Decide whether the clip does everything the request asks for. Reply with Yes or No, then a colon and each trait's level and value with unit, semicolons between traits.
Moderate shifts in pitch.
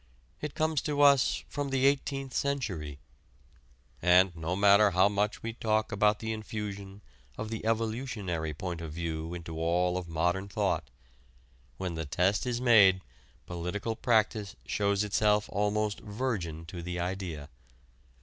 Yes: average, 4.1 semitones